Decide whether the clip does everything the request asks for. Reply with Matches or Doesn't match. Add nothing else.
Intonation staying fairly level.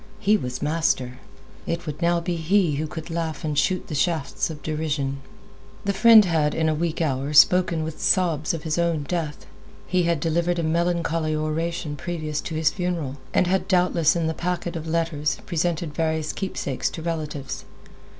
Matches